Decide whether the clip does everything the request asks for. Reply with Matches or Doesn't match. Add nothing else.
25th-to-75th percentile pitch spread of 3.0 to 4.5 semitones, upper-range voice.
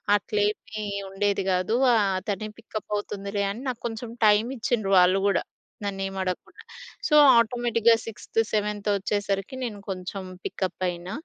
Doesn't match